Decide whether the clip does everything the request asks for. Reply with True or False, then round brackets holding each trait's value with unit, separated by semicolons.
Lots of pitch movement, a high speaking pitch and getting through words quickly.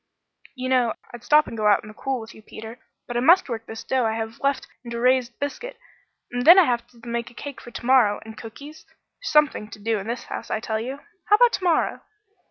False (3.8 semitones; 240 Hz; 250 wpm)